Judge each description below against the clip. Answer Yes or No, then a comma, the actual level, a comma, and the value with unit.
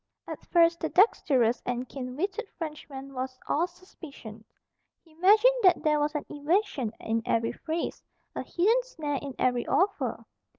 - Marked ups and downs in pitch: Yes, wide, 5.9 semitones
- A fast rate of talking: No, average, 155 wpm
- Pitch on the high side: Yes, very high, 305 Hz